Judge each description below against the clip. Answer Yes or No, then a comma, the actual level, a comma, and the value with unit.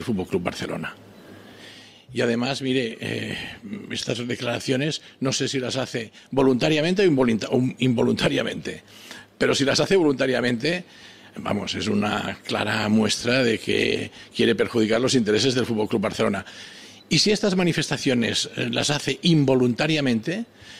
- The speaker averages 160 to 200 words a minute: No, slow, 135 wpm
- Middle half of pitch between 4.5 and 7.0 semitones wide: No, average, 3.4 semitones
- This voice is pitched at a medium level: No, low, 130 Hz